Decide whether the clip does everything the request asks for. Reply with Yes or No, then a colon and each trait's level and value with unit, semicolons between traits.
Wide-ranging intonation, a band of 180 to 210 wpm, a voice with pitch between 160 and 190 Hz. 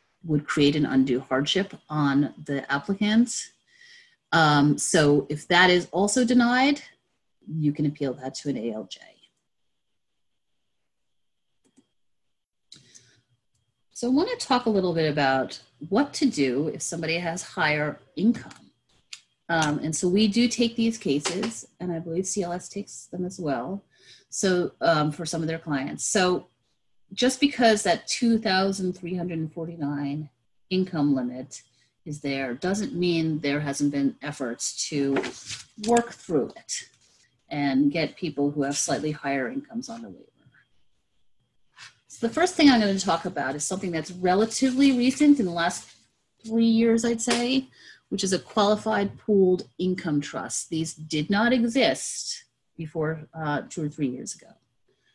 No: wide, 6.7 semitones; average, 145 wpm; medium, 165 Hz